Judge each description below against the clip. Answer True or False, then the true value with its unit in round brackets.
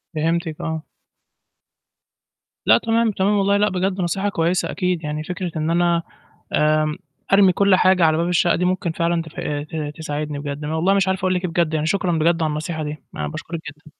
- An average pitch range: True (3.0 semitones)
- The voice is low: False (170 Hz)